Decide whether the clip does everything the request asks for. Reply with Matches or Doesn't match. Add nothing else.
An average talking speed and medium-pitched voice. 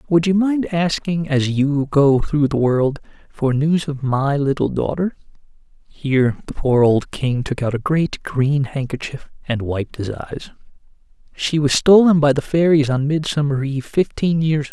Matches